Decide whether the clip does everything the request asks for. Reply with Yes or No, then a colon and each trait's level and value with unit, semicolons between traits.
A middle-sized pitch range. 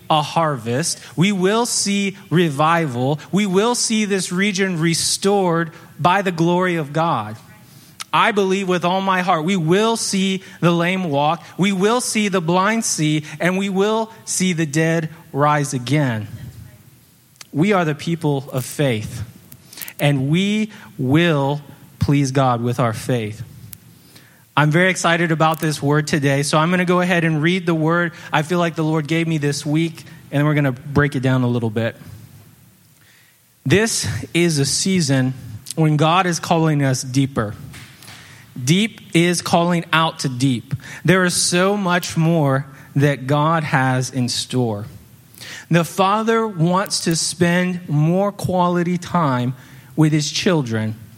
Yes: average, 4.6 semitones